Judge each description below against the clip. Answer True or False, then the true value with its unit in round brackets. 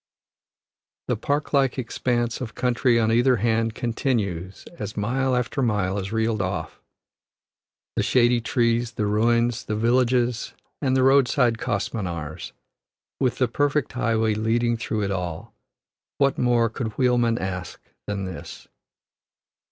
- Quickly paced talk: False (135 wpm)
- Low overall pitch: True (115 Hz)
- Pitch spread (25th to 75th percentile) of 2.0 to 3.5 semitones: True (2.8 semitones)